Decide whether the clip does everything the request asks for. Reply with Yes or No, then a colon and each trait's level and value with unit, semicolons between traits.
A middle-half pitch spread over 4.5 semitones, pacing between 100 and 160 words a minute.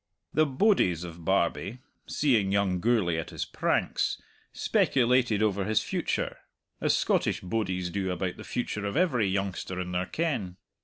Yes: average, 4.9 semitones; average, 150 wpm